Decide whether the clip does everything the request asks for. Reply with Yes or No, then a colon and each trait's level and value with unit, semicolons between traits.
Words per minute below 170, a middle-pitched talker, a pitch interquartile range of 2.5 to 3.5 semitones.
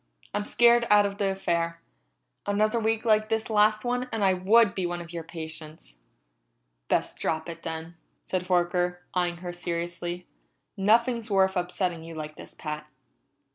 No: average, 160 wpm; medium, 180 Hz; average, 4.0 semitones